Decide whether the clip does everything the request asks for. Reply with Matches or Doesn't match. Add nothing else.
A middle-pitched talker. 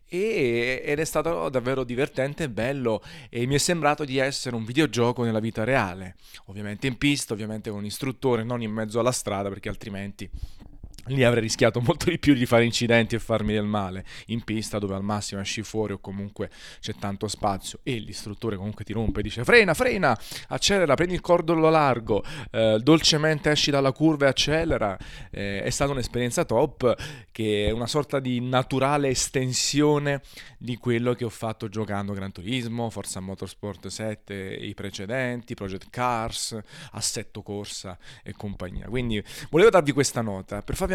Doesn't match